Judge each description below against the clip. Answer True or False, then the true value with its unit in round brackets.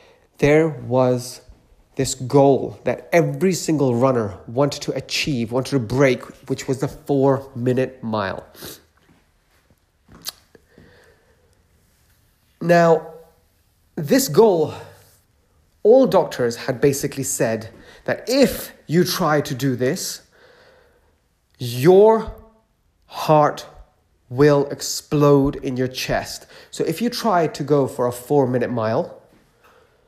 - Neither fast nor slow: False (105 wpm)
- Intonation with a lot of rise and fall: False (4.8 semitones)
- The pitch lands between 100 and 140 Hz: True (135 Hz)